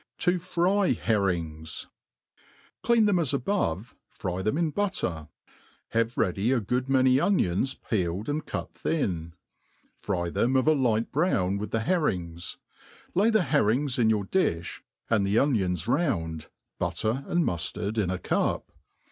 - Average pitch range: No, wide, 8.6 semitones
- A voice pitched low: Yes, low, 115 Hz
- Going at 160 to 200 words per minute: No, average, 140 wpm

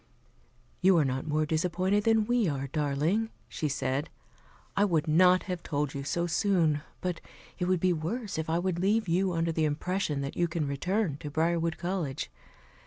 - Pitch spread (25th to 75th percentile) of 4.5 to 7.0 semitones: No, average, 3.7 semitones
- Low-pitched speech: No, medium, 170 Hz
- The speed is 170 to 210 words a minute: Yes, average, 180 wpm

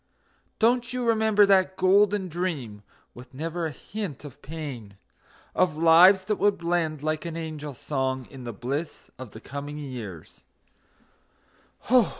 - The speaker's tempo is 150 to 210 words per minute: No, average, 140 wpm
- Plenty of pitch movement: Yes, wide, 5.9 semitones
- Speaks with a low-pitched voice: No, medium, 160 Hz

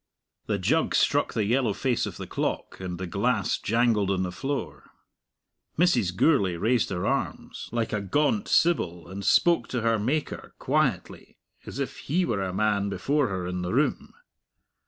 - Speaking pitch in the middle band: No, low, 105 Hz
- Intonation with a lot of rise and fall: Yes, wide, 5.9 semitones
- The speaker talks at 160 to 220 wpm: Yes, average, 170 wpm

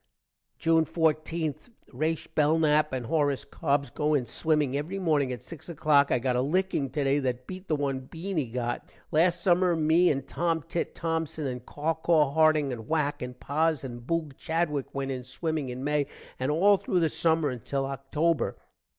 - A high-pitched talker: No, medium, 150 Hz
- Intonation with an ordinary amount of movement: Yes, average, 3.2 semitones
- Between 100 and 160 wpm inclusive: No, average, 170 wpm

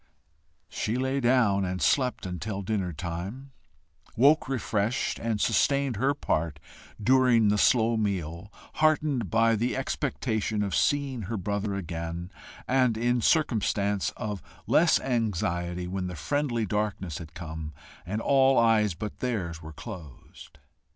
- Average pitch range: No, wide, 5.7 semitones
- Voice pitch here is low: Yes, low, 105 Hz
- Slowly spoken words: Yes, slow, 130 wpm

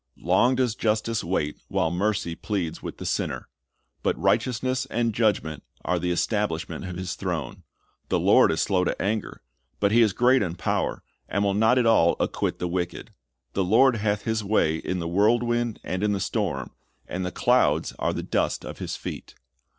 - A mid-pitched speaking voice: No, low, 100 Hz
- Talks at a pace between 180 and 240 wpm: Yes, average, 185 wpm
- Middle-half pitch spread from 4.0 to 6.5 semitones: Yes, average, 4.3 semitones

